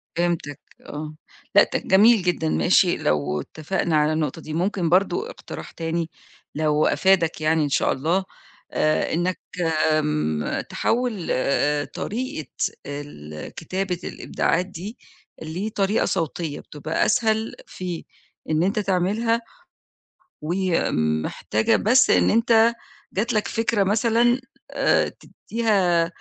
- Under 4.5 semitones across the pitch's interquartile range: No, wide, 5.5 semitones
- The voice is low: No, medium, 175 Hz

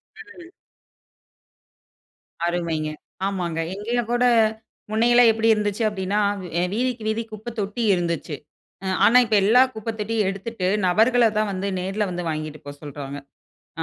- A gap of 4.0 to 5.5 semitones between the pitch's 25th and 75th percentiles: Yes, average, 4.3 semitones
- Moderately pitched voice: No, high, 205 Hz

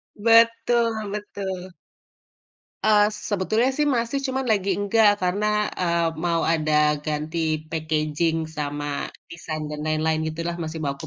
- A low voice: No, medium, 170 Hz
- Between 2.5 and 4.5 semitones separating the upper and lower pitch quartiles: No, average, 5.3 semitones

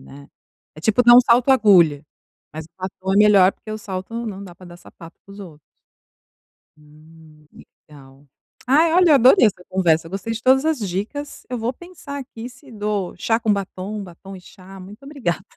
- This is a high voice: Yes, high, 200 Hz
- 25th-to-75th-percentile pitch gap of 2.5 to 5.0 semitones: No, wide, 5.5 semitones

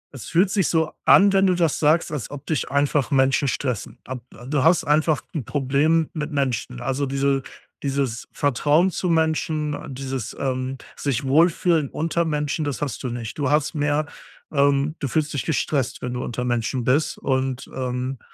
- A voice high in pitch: No, medium, 140 Hz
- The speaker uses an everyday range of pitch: Yes, average, 3.0 semitones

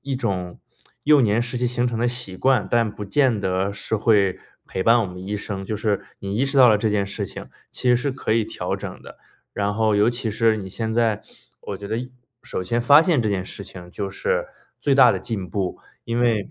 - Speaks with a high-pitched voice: No, low, 110 Hz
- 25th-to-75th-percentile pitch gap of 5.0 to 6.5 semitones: No, average, 3.4 semitones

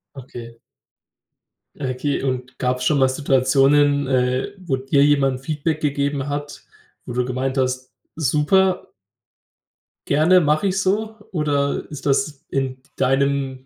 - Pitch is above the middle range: No, medium, 140 Hz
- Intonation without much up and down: Yes, narrow, 2.3 semitones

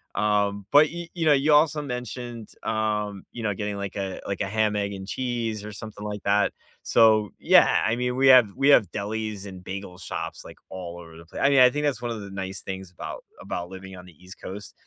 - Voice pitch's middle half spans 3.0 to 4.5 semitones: Yes, average, 3.9 semitones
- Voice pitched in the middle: No, low, 105 Hz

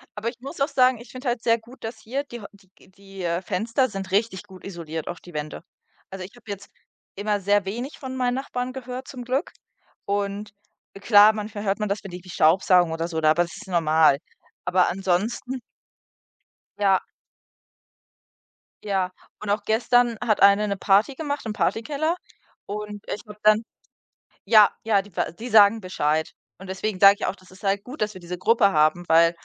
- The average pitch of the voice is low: No, high, 205 Hz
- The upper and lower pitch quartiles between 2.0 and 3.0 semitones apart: No, average, 3.8 semitones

